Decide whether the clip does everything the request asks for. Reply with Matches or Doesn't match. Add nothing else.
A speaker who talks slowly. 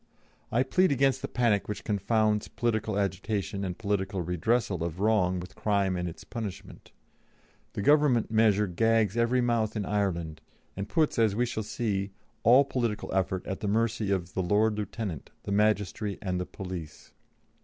Doesn't match